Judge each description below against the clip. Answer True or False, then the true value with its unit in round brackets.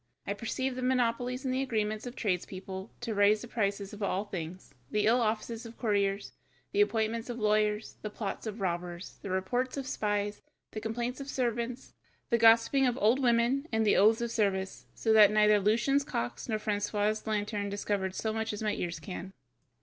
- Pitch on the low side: False (215 Hz)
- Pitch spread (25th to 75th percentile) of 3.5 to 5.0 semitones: False (2.7 semitones)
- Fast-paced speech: False (190 wpm)